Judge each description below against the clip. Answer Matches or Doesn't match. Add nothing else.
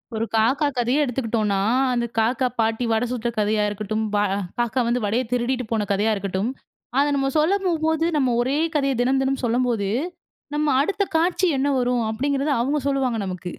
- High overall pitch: Matches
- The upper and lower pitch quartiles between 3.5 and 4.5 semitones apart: Matches